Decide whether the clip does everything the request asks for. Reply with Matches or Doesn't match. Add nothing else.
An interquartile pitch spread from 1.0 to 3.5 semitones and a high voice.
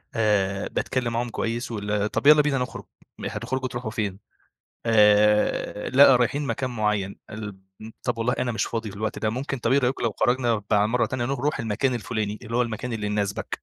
Doesn't match